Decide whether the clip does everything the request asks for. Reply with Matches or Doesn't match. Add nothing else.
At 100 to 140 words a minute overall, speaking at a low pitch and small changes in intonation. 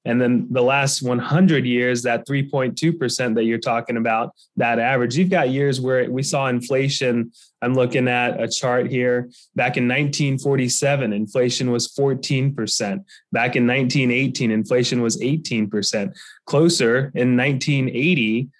Matches